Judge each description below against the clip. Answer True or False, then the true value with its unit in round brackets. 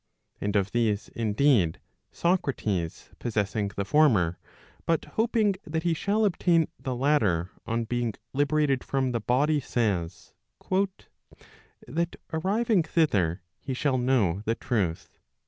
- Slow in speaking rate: True (125 wpm)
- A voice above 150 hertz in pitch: False (125 Hz)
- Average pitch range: False (7.3 semitones)